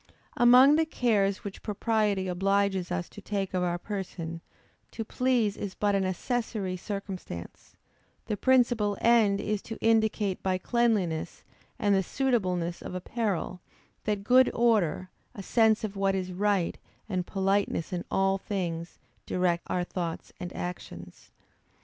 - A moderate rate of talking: Yes, average, 145 wpm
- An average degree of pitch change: Yes, average, 3.2 semitones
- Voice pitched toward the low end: No, high, 195 Hz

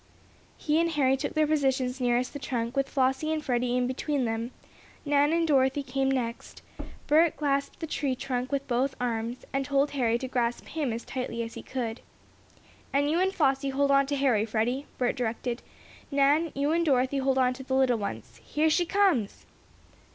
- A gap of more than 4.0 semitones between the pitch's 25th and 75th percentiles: No, average, 2.7 semitones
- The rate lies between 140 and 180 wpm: No, average, 190 wpm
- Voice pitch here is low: No, very high, 270 Hz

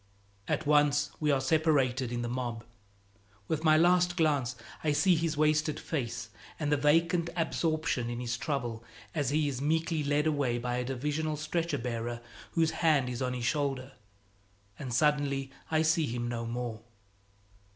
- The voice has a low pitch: No, medium, 145 Hz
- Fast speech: No, average, 160 wpm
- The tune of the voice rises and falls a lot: No, average, 4.0 semitones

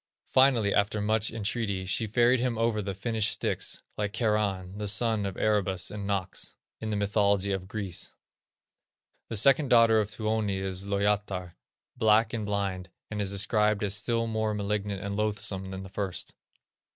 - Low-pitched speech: Yes, low, 105 Hz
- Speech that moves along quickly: No, average, 165 wpm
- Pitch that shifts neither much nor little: No, narrow, 1.9 semitones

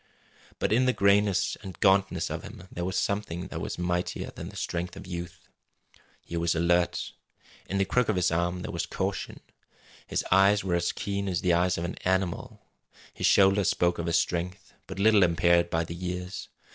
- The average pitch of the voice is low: Yes, very low, 90 Hz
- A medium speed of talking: Yes, average, 195 wpm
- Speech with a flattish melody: Yes, narrow, 2.1 semitones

